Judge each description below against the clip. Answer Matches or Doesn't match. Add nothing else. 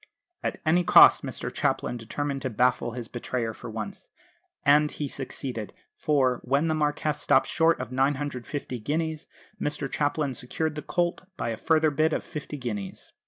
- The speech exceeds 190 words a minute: Doesn't match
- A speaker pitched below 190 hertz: Matches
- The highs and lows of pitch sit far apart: Doesn't match